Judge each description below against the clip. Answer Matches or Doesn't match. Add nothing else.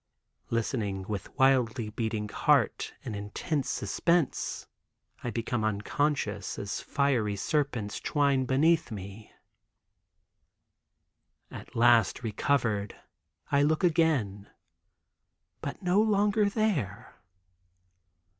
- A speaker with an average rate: Doesn't match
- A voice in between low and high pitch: Doesn't match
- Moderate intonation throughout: Doesn't match